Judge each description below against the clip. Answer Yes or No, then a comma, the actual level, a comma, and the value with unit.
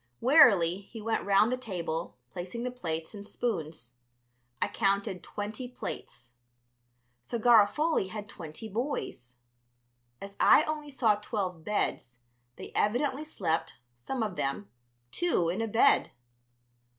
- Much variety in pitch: Yes, wide, 6.3 semitones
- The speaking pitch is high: Yes, high, 205 Hz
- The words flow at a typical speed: No, slow, 125 wpm